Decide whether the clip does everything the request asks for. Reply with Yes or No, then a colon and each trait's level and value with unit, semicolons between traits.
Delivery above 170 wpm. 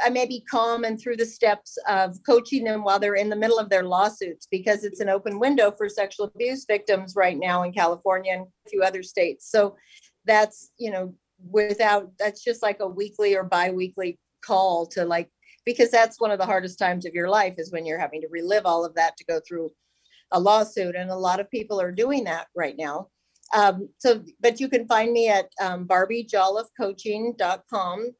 Yes: fast, 205 wpm